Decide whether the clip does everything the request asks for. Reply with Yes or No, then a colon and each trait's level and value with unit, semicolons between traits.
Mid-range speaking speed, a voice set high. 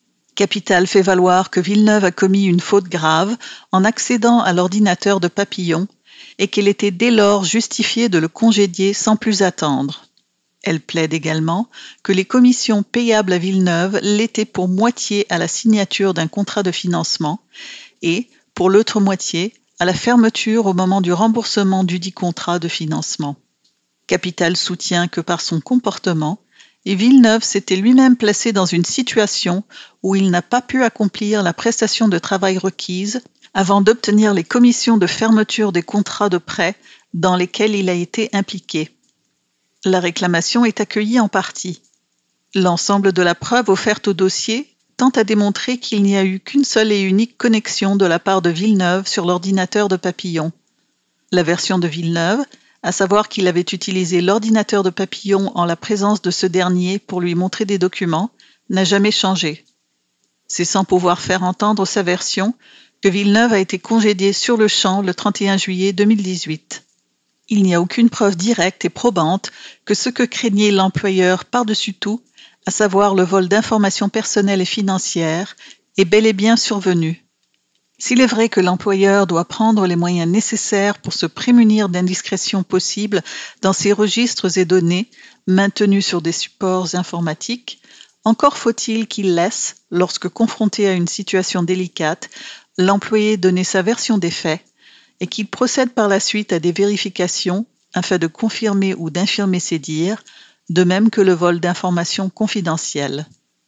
Yes: average, 160 wpm; high, 195 Hz